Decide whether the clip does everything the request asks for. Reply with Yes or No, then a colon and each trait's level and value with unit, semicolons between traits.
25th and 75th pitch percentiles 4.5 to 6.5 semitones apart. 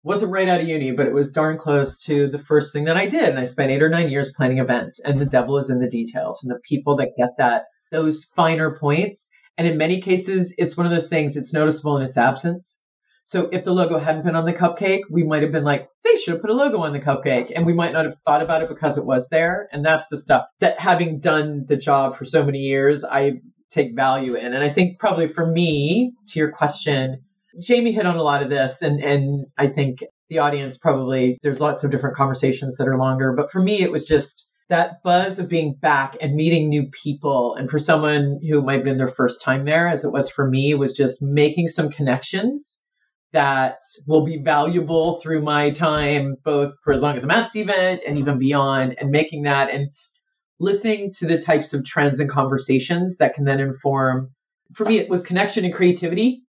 No: average, 3.6 semitones